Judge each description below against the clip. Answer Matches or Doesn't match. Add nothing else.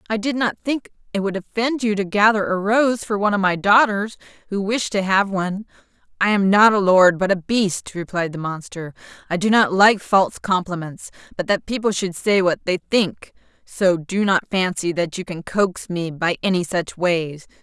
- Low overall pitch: Doesn't match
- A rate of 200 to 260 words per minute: Matches